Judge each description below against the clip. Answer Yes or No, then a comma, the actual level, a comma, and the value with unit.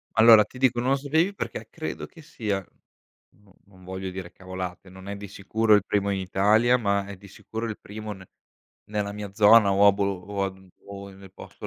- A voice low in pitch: Yes, low, 100 Hz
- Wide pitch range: No, narrow, 2.4 semitones